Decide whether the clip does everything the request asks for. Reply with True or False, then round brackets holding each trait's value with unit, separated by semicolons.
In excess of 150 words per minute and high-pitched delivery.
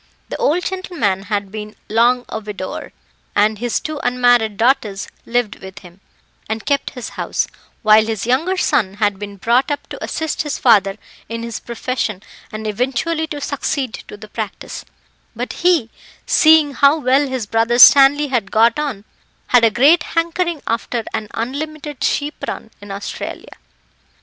True (160 wpm; 240 Hz)